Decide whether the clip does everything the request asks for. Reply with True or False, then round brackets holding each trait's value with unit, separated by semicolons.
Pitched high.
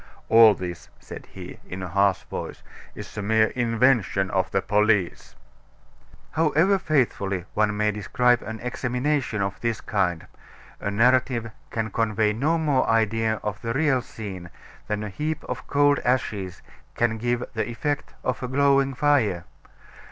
False (115 Hz)